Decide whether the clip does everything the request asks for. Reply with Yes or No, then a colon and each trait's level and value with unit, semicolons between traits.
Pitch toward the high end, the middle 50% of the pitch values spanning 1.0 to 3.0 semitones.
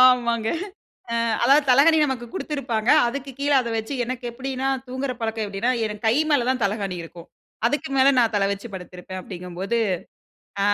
No: high, 235 Hz; average, 4.4 semitones